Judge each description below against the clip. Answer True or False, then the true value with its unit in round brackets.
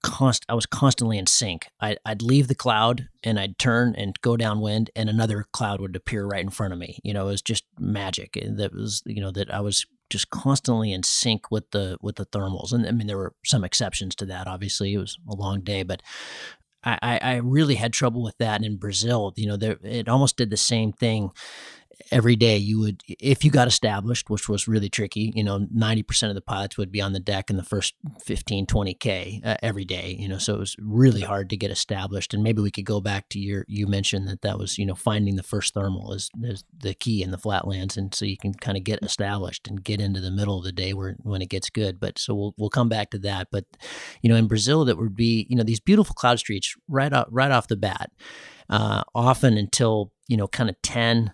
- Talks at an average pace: False (240 wpm)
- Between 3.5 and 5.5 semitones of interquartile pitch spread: False (2.7 semitones)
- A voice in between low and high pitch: False (105 Hz)